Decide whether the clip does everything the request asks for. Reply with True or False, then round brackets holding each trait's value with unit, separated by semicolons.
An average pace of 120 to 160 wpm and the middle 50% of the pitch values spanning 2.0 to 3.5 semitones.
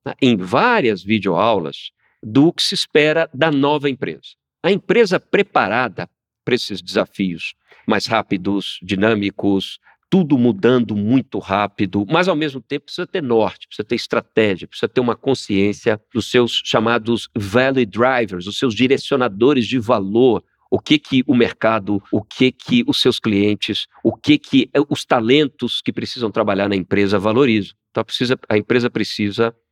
False (150 wpm; 4.5 semitones)